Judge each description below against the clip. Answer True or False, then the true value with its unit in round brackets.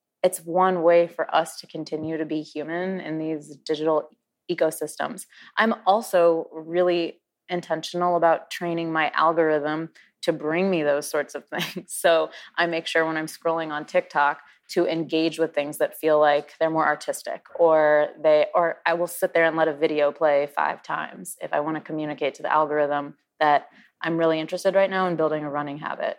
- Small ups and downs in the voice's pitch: True (2.0 semitones)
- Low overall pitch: False (160 Hz)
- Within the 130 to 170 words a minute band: False (185 wpm)